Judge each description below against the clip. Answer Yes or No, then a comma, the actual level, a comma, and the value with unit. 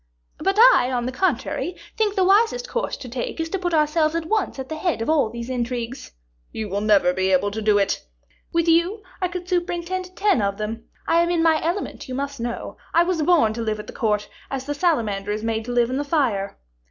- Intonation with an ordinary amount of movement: No, wide, 7.5 semitones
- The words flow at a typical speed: No, fast, 235 wpm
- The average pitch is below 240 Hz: No, very high, 280 Hz